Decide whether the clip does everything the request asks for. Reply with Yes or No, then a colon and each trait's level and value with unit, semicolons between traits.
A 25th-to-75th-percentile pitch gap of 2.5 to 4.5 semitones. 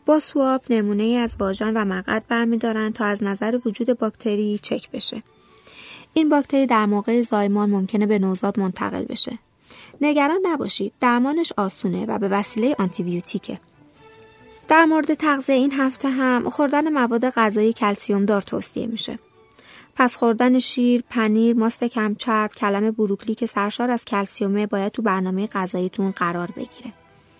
Yes: average, 3.6 semitones